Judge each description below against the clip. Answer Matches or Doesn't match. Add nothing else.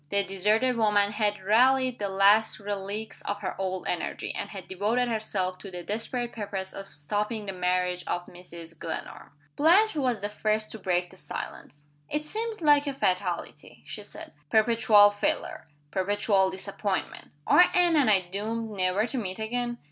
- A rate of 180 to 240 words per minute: Doesn't match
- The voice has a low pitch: Doesn't match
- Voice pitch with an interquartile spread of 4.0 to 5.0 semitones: Doesn't match